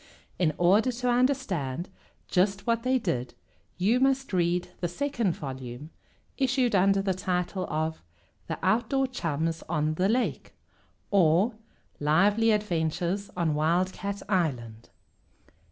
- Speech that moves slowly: Yes, slow, 120 wpm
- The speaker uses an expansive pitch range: Yes, wide, 5.9 semitones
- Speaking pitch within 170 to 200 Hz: Yes, medium, 185 Hz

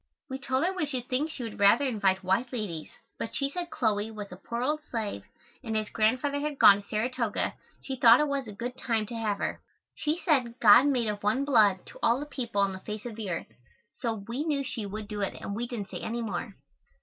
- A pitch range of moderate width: Yes, average, 4.3 semitones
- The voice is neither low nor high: No, high, 230 Hz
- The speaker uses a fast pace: Yes, fast, 235 wpm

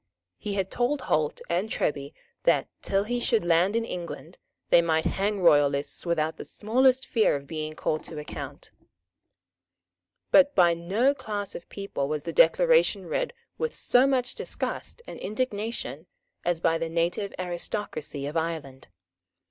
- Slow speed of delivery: No, average, 150 wpm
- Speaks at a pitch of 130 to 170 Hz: No, medium, 180 Hz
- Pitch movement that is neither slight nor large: No, wide, 6.3 semitones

